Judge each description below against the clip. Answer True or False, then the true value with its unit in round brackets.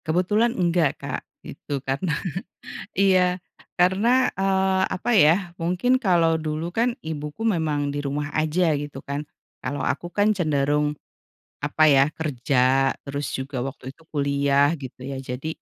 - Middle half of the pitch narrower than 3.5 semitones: False (4.4 semitones)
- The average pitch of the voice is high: False (155 Hz)